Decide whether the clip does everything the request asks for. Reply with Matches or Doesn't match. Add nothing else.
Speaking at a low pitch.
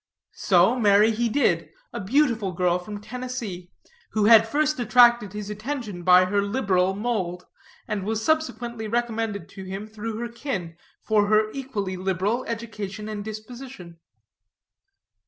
Doesn't match